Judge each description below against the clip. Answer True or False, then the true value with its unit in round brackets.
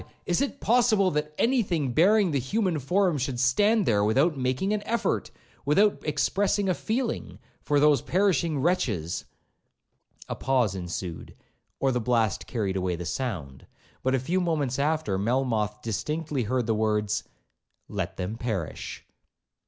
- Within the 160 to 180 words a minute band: False (145 wpm)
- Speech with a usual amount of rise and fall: False (8.7 semitones)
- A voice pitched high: False (135 Hz)